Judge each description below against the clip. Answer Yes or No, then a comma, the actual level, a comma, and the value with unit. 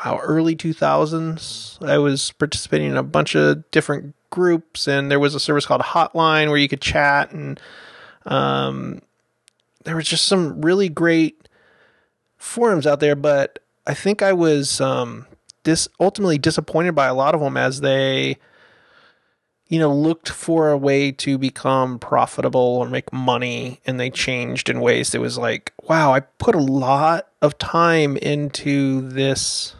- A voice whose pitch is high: No, medium, 140 Hz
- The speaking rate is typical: Yes, average, 160 wpm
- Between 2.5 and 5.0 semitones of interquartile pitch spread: Yes, average, 4.1 semitones